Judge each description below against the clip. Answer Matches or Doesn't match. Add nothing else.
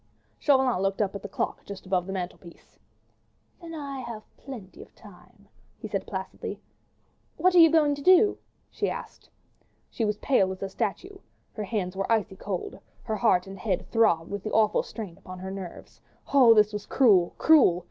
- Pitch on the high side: Matches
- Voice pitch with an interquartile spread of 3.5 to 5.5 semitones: Matches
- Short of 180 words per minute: Doesn't match